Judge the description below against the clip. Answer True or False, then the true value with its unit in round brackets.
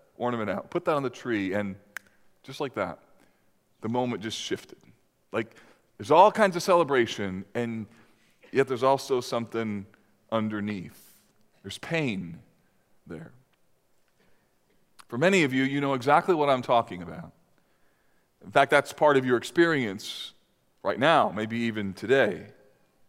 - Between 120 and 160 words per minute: True (140 wpm)